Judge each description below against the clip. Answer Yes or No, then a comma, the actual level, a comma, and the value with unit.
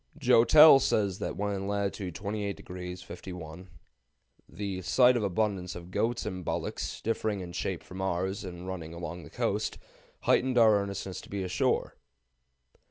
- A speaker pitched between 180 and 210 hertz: No, very low, 95 Hz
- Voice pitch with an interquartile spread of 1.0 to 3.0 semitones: Yes, narrow, 2.5 semitones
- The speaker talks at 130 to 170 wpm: Yes, average, 150 wpm